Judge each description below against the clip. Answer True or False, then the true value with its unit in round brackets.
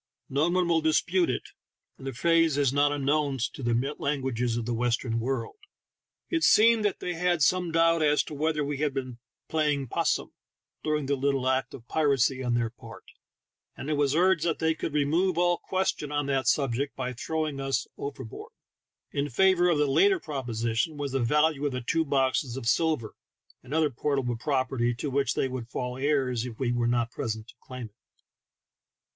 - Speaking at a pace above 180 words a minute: True (195 wpm)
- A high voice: False (140 Hz)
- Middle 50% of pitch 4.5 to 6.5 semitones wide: False (3.9 semitones)